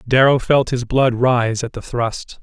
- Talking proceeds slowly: No, average, 200 wpm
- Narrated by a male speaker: Yes, male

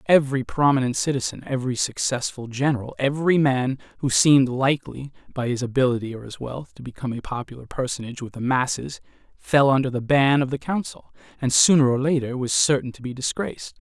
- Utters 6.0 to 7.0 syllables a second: Yes, 6.1 syllables/s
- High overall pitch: No, low, 135 Hz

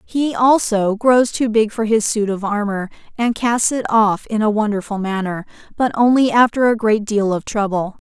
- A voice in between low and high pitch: No, high, 220 Hz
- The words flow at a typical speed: Yes, average, 195 wpm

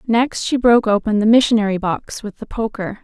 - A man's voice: No, female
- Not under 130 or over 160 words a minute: No, average, 200 wpm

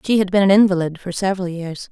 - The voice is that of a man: No, female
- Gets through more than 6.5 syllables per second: Yes, 6.8 syllables/s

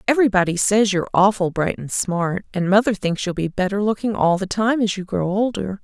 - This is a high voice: Yes, high, 195 Hz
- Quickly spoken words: Yes, fast, 215 wpm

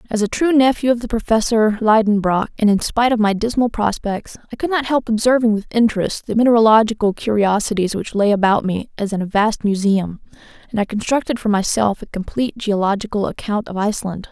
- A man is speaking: No, female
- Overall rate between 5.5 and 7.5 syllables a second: Yes, 5.9 syllables/s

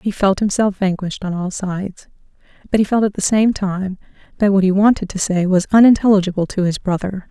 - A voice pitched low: No, high, 195 Hz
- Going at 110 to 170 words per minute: No, fast, 205 wpm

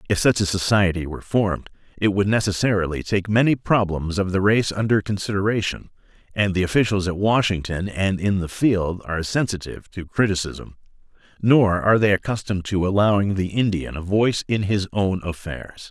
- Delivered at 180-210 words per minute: No, average, 165 wpm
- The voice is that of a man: Yes, male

